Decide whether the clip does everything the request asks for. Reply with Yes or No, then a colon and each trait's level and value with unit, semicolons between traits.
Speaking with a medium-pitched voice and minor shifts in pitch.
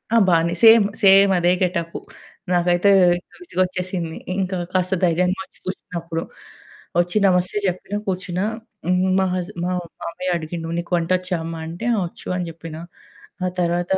Yes: medium, 180 Hz; narrow, 1.5 semitones